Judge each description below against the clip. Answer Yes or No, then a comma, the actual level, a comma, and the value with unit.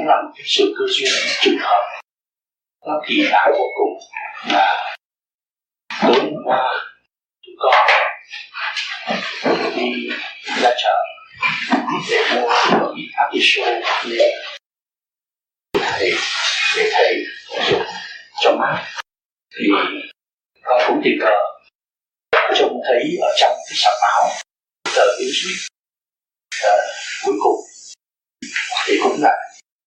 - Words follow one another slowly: Yes, slow, 115 wpm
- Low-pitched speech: No, very high, 390 Hz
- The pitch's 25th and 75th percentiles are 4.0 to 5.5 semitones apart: No, narrow, 2.6 semitones